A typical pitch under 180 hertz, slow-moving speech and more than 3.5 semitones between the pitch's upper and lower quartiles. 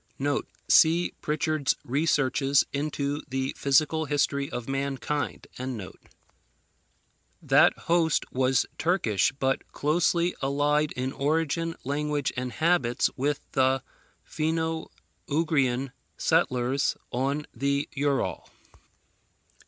No: medium, 140 Hz; slow, 90 wpm; average, 2.7 semitones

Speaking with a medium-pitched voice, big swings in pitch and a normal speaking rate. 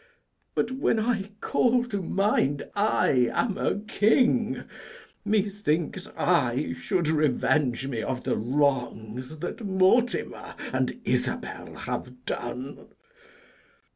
No: medium, 170 Hz; wide, 8.7 semitones; slow, 105 wpm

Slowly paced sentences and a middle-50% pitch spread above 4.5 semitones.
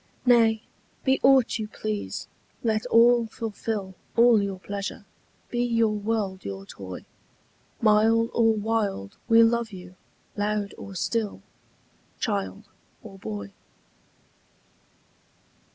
No: slow, 105 wpm; narrow, 2.5 semitones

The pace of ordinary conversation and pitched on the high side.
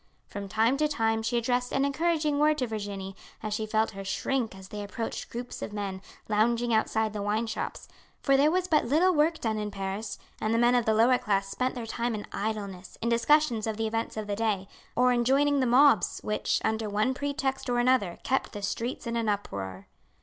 No: fast, 215 wpm; high, 225 Hz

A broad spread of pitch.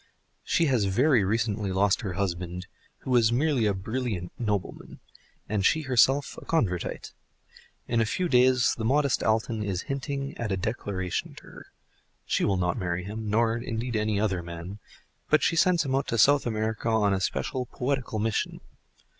No: average, 4.6 semitones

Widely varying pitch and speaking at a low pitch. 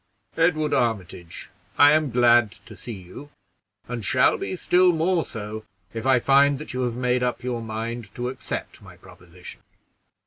No: average, 4.2 semitones; low, 125 Hz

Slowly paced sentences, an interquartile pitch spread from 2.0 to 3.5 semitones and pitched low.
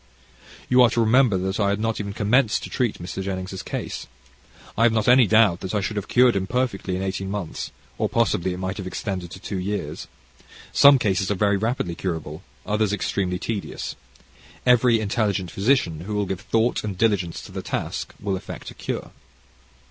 No: average, 195 wpm; average, 3.1 semitones; low, 100 Hz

